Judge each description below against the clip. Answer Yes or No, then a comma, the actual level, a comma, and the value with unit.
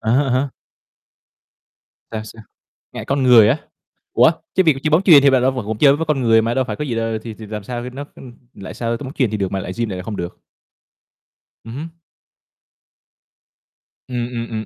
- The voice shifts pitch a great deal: No, average, 3.8 semitones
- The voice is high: No, low, 120 Hz